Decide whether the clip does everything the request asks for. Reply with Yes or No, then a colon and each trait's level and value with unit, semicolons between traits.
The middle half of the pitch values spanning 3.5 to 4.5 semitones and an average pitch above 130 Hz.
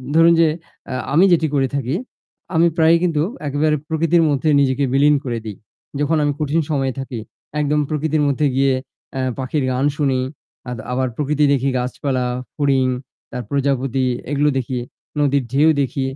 No: narrow, 2.4 semitones; medium, 140 Hz